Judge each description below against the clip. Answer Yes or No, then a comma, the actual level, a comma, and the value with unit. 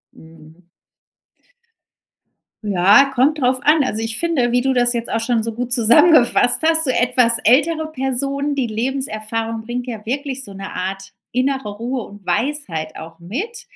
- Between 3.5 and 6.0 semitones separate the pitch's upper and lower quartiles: Yes, average, 4.2 semitones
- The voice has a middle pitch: No, high, 245 Hz